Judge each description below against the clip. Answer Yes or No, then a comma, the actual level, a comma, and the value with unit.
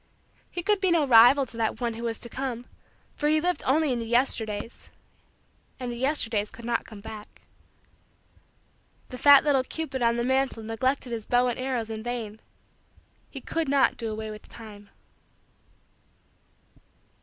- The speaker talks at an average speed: Yes, average, 165 wpm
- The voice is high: Yes, high, 240 Hz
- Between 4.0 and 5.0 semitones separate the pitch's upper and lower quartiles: No, average, 3.2 semitones